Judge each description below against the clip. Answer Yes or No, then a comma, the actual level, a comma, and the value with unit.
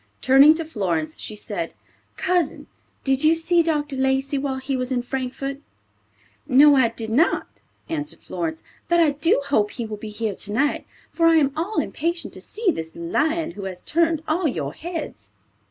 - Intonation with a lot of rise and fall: Yes, wide, 6.2 semitones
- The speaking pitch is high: Yes, very high, 275 Hz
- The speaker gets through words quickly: No, average, 175 wpm